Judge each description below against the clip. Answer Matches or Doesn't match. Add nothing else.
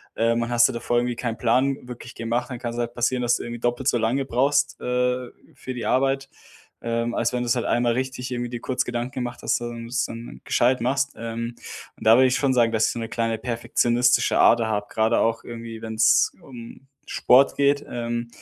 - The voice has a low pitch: Matches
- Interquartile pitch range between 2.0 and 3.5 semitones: Doesn't match